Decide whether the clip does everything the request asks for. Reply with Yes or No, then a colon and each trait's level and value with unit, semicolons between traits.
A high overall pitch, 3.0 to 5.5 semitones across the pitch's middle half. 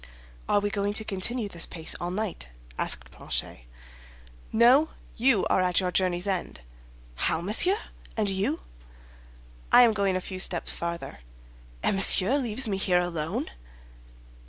Yes: high, 195 Hz; average, 3.6 semitones